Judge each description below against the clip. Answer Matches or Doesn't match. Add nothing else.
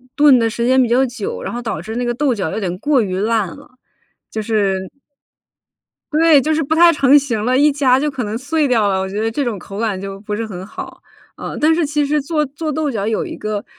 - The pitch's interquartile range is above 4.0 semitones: Matches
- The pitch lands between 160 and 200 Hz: Doesn't match